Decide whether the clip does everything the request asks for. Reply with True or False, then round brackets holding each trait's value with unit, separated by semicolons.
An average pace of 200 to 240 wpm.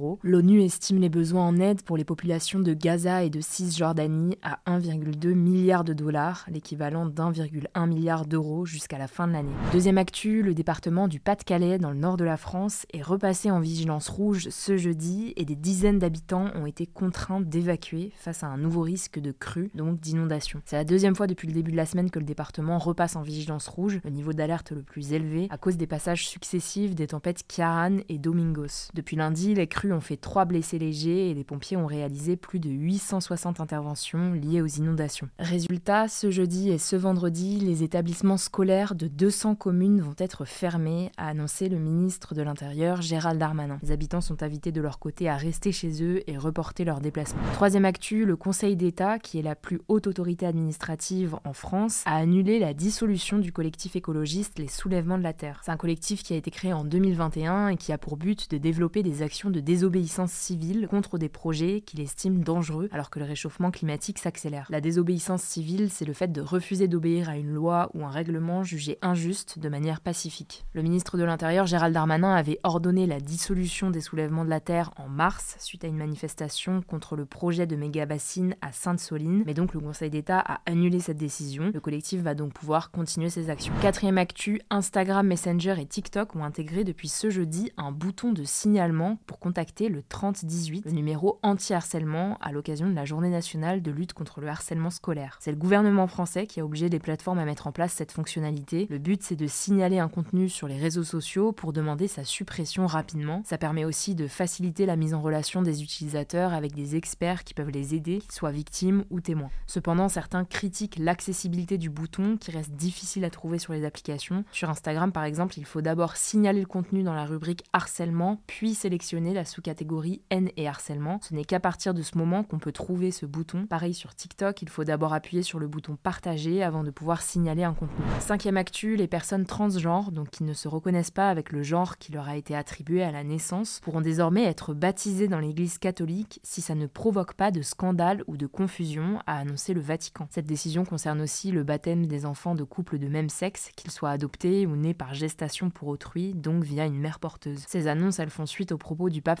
True (205 wpm)